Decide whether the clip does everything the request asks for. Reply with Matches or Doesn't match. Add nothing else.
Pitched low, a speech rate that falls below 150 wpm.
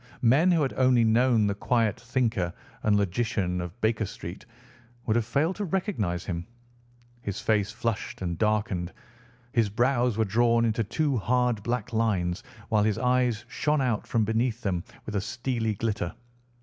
Doesn't match